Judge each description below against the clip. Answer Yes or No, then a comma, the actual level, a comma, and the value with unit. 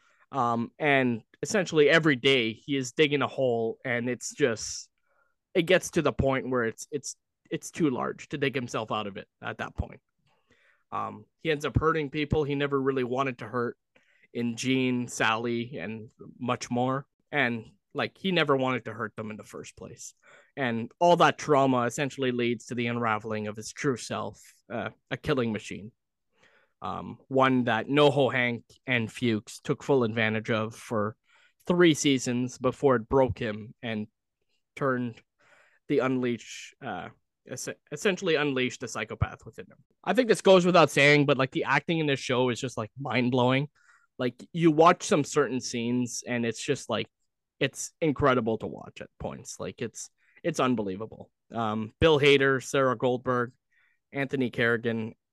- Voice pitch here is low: Yes, low, 130 Hz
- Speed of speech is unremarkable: Yes, average, 165 wpm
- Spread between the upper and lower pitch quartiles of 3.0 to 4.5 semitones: Yes, average, 3.5 semitones